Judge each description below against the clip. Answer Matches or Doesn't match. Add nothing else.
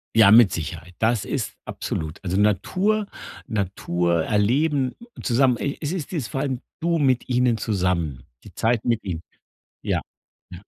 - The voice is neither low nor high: Doesn't match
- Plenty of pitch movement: Matches